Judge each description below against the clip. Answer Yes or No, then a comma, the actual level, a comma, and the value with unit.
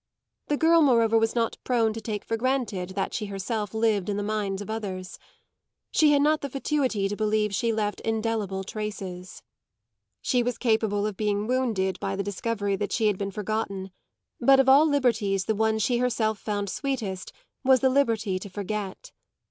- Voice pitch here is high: Yes, high, 215 Hz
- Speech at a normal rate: Yes, average, 180 wpm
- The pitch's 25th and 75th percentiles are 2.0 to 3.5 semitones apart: Yes, average, 3.1 semitones